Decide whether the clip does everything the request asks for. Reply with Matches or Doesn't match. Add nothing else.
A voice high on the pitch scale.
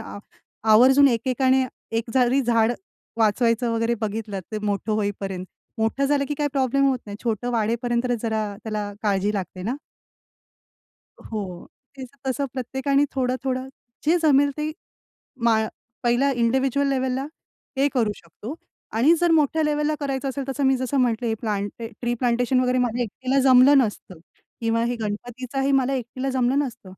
Matches